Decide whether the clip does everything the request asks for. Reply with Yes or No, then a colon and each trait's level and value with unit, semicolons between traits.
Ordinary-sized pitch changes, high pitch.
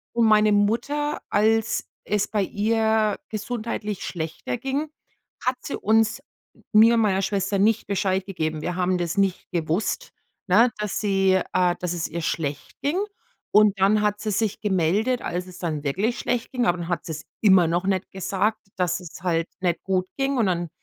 Yes: average, 3.6 semitones; high, 195 Hz